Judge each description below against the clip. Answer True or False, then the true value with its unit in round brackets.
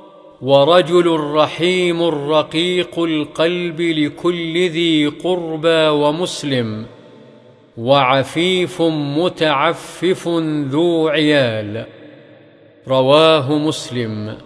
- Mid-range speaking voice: True (155 Hz)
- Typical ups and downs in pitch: True (3.0 semitones)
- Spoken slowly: True (60 wpm)